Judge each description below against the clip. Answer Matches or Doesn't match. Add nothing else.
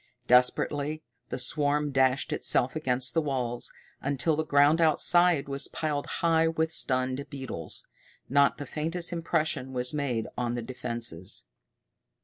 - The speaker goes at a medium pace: Doesn't match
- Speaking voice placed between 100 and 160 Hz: Matches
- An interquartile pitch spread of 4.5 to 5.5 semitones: Doesn't match